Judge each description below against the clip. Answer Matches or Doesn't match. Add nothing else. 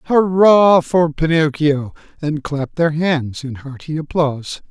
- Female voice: Doesn't match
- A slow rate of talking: Matches